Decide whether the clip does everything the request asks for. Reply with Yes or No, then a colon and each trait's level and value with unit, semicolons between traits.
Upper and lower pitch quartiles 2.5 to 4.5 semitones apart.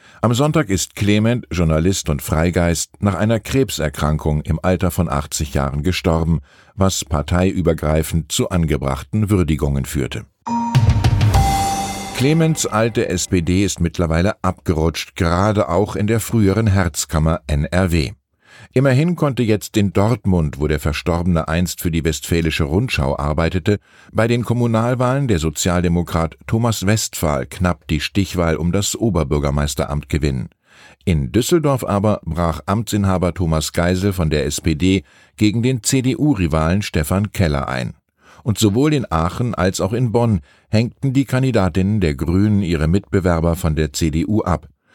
No: average, 5.0 semitones